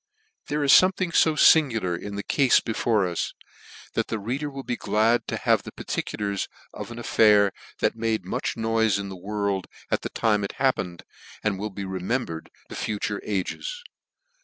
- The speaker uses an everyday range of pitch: Yes, average, 3.5 semitones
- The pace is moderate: Yes, average, 180 wpm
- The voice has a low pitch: Yes, low, 110 Hz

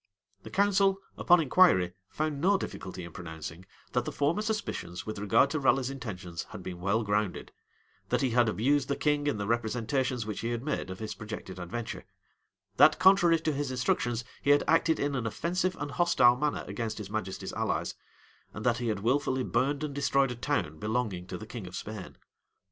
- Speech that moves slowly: No, average, 195 wpm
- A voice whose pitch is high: No, low, 120 Hz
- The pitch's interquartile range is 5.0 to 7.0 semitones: Yes, wide, 5.5 semitones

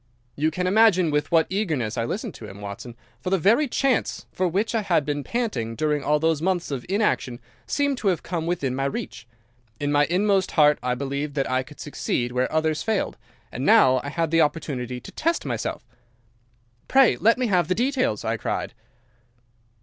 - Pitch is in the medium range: Yes, medium, 160 Hz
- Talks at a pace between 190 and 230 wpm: Yes, average, 195 wpm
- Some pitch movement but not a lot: No, wide, 6.0 semitones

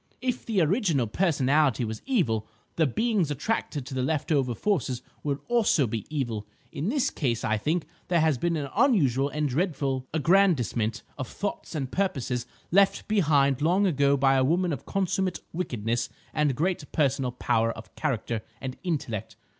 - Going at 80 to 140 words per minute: No, average, 165 wpm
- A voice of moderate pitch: Yes, medium, 145 Hz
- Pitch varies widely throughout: Yes, wide, 5.9 semitones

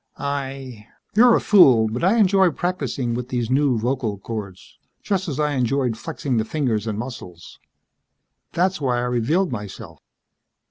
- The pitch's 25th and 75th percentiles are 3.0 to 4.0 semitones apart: No, average, 5.3 semitones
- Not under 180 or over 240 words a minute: No, average, 155 wpm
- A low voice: Yes, low, 130 Hz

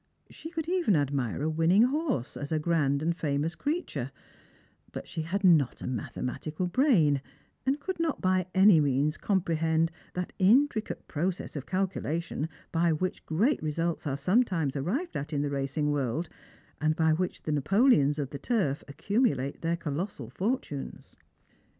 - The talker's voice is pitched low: No, medium, 165 Hz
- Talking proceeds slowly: No, average, 155 wpm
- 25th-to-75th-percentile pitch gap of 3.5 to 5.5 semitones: Yes, average, 5.2 semitones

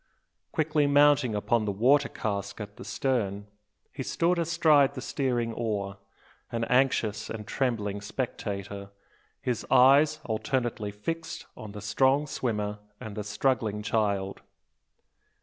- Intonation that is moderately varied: Yes, average, 4.9 semitones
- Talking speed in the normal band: No, slow, 125 wpm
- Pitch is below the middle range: Yes, low, 115 Hz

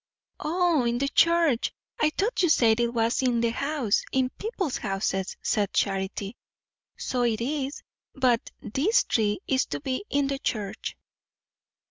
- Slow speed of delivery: No, average, 150 wpm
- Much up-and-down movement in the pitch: No, average, 4.9 semitones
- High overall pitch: Yes, very high, 255 Hz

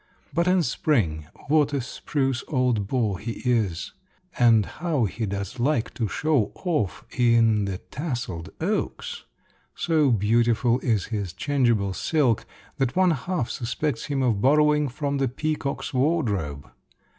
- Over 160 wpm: No, slow, 135 wpm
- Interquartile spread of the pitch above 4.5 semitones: Yes, wide, 5.5 semitones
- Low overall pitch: Yes, low, 125 Hz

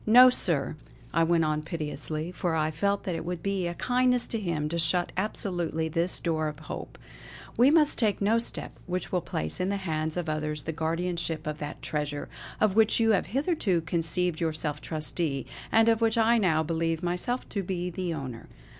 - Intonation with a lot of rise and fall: No, average, 4.2 semitones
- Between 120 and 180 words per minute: No, average, 195 wpm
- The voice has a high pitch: No, medium, 170 Hz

